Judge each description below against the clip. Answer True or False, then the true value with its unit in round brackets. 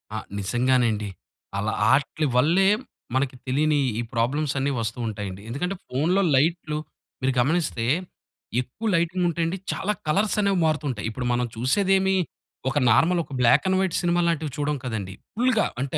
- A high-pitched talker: False (145 Hz)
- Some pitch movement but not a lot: False (6.0 semitones)